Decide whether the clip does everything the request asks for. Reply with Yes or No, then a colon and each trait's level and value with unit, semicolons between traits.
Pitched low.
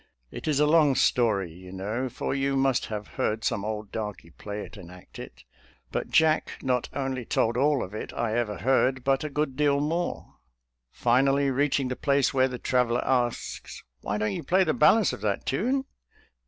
Yes: low, 130 Hz